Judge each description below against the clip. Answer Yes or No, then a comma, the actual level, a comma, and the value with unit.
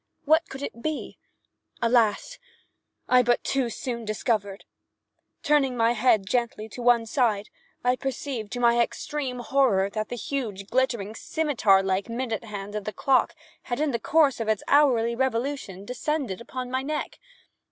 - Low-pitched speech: No, high, 240 Hz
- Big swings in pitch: No, average, 3.7 semitones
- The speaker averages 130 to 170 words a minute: Yes, average, 155 wpm